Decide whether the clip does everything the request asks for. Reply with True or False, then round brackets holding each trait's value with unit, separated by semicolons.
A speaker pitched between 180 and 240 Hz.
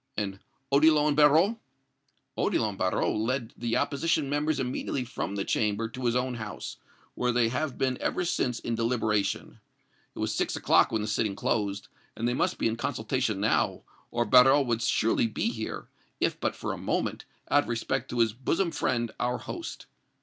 False (120 Hz)